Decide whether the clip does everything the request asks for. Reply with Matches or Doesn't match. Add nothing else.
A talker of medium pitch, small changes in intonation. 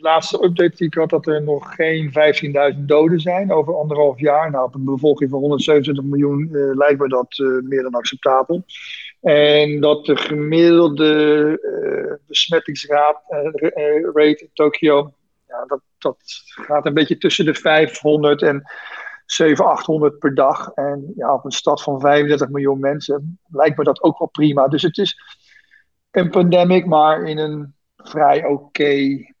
Matches